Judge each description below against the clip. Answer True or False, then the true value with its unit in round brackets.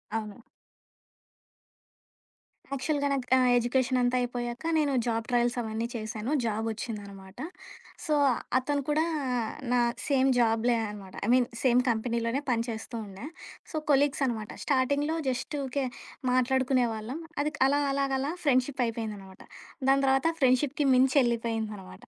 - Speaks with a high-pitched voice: True (245 Hz)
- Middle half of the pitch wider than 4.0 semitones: False (3.2 semitones)